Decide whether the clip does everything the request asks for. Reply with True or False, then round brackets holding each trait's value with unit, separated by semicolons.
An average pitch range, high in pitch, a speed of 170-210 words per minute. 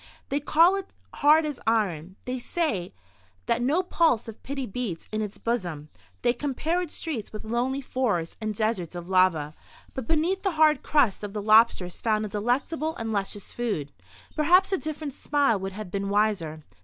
False (7.0 semitones; 230 Hz; 180 wpm)